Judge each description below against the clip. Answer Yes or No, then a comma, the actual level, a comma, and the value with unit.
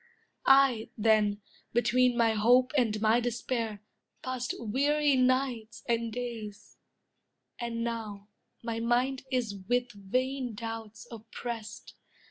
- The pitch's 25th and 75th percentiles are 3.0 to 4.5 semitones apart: No, narrow, 2.5 semitones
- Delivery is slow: Yes, slow, 105 wpm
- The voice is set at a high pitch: Yes, high, 235 Hz